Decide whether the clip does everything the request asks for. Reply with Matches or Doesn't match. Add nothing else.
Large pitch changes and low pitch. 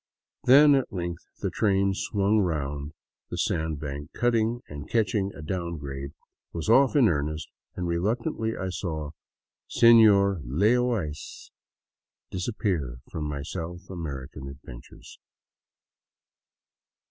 Matches